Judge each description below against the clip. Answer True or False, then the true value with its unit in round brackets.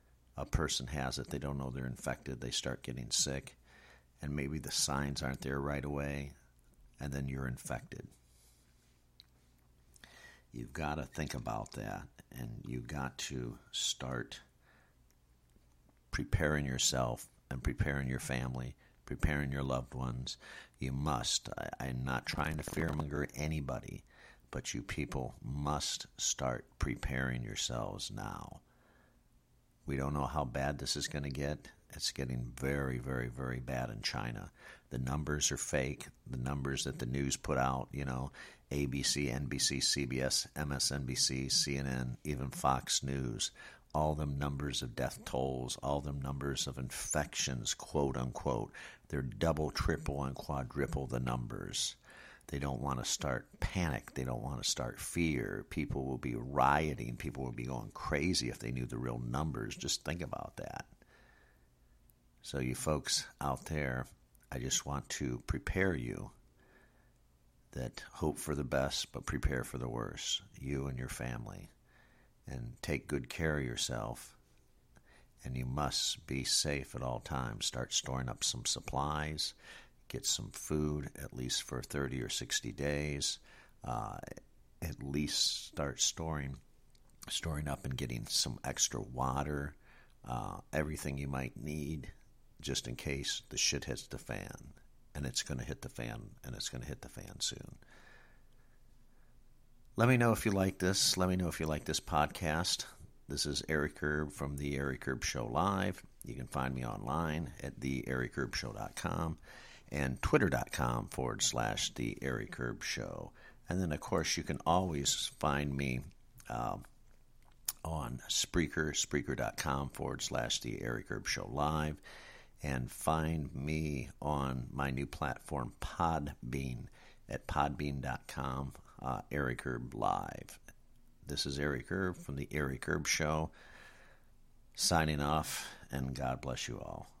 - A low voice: True (70 Hz)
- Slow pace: False (145 wpm)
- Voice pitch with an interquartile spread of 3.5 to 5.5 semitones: False (2.7 semitones)